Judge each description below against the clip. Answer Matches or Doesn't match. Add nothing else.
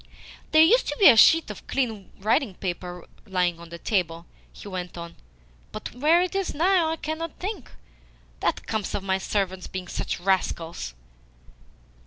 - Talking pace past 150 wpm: Matches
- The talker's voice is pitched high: Matches